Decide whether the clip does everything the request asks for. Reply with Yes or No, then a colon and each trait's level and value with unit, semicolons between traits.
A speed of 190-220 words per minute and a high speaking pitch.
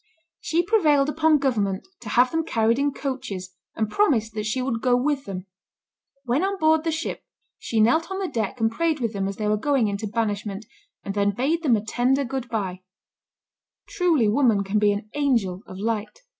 Yes: average, 200 wpm; high, 235 Hz